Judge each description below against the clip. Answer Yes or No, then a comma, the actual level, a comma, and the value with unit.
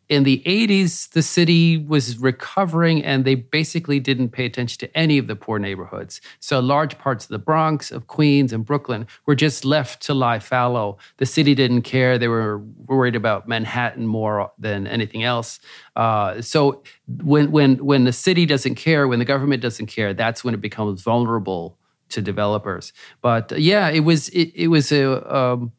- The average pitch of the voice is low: Yes, low, 130 Hz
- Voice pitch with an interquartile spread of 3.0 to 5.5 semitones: Yes, average, 4.5 semitones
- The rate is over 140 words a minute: Yes, average, 185 wpm